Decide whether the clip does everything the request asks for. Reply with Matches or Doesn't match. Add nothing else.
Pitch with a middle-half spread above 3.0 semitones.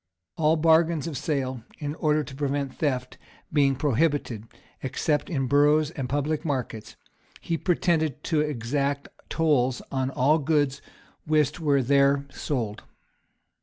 Doesn't match